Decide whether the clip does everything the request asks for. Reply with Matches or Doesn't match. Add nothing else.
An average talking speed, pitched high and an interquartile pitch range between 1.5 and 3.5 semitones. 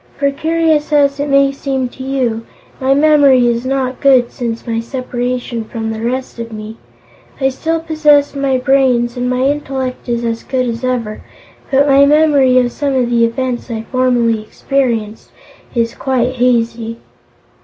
Matches